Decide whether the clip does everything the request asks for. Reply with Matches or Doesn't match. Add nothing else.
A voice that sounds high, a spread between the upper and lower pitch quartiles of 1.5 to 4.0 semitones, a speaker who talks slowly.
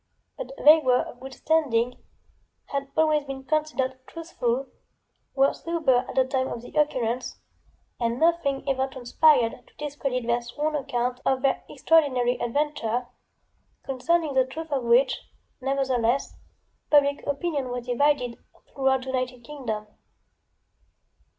Matches